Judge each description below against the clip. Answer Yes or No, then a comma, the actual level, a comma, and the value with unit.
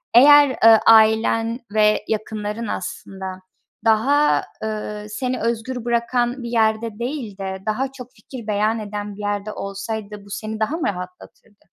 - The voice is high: Yes, high, 220 Hz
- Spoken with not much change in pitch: Yes, narrow, 2.3 semitones